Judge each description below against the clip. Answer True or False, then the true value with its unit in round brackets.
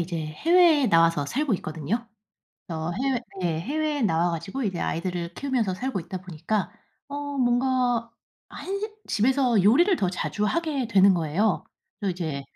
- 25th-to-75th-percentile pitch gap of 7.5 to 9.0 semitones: True (7.8 semitones)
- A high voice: True (210 Hz)